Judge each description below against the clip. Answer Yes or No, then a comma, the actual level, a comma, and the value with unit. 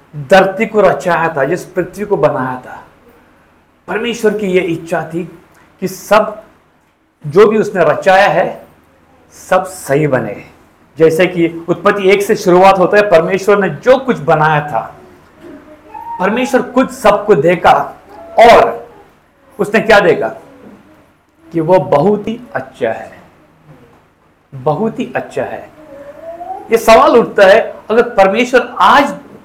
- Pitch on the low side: No, high, 195 Hz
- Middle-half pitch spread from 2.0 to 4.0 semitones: No, average, 5.0 semitones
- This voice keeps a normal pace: Yes, average, 130 wpm